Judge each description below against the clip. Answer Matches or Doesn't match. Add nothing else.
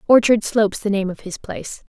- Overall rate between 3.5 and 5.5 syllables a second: Doesn't match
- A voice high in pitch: Matches